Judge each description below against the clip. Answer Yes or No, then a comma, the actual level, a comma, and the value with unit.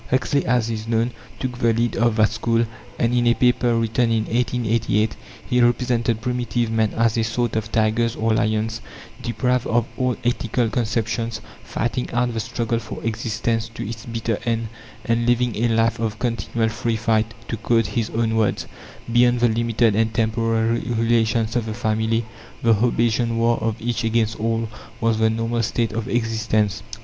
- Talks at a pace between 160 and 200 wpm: Yes, average, 175 wpm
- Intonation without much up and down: Yes, narrow, 1.1 semitones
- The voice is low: Yes, low, 115 Hz